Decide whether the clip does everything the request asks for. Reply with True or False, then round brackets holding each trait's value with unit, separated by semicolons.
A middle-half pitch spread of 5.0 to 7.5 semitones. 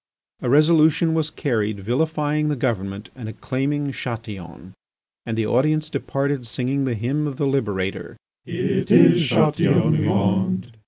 True (5.5 semitones)